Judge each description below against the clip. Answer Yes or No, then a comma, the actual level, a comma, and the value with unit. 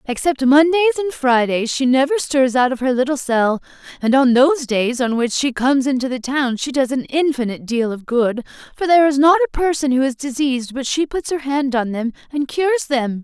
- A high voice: Yes, very high, 270 Hz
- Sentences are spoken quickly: Yes, fast, 220 wpm